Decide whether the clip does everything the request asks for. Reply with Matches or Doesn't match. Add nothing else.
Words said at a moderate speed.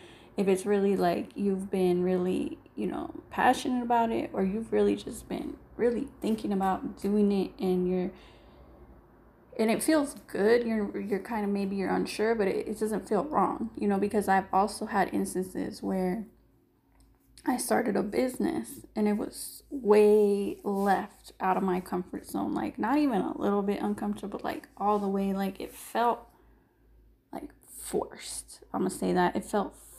Matches